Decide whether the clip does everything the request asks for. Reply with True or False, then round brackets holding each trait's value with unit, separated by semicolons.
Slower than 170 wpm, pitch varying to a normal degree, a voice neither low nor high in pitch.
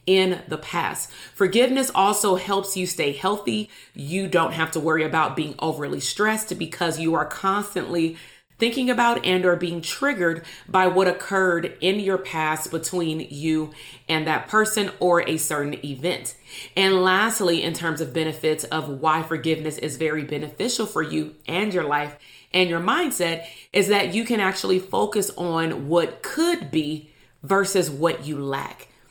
True (160 wpm; 3.5 semitones; 170 Hz)